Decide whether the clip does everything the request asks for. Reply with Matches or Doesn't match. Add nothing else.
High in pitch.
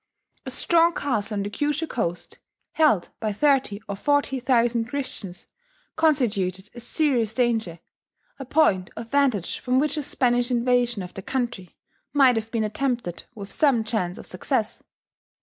Matches